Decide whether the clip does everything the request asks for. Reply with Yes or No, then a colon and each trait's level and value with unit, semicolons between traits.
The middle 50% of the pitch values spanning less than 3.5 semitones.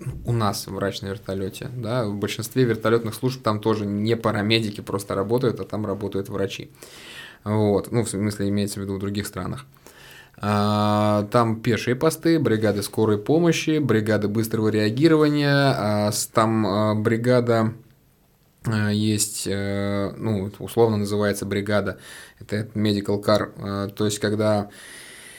Yes: narrow, 2.5 semitones